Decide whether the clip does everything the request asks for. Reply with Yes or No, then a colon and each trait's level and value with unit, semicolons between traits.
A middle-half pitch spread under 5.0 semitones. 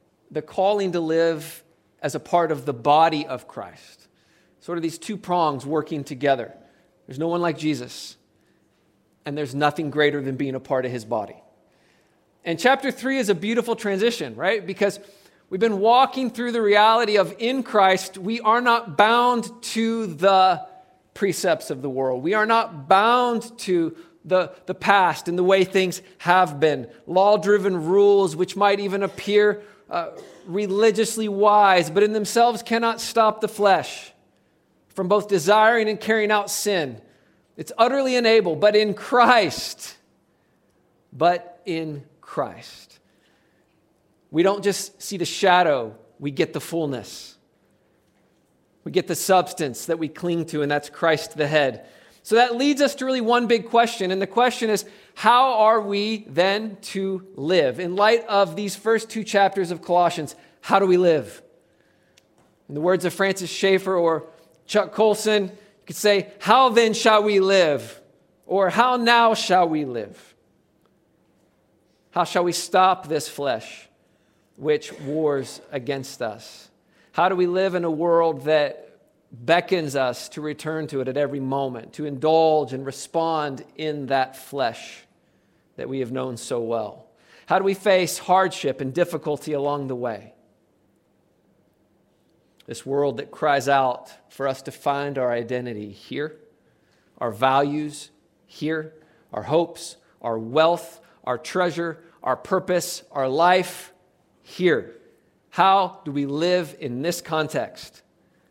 No: average, 5.3 semitones